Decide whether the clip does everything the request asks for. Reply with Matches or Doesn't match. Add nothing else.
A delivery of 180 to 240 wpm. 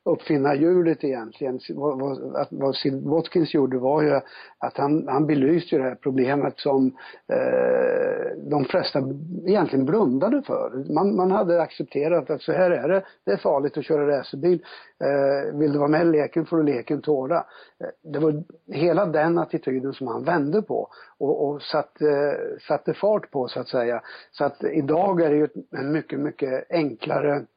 Doesn't match